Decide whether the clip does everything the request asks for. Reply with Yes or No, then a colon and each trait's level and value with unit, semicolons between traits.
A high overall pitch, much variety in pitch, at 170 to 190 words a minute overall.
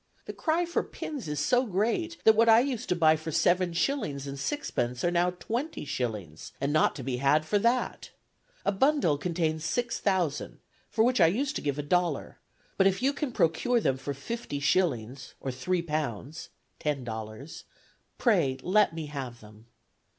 No: medium, 165 Hz; wide, 8.6 semitones; average, 180 wpm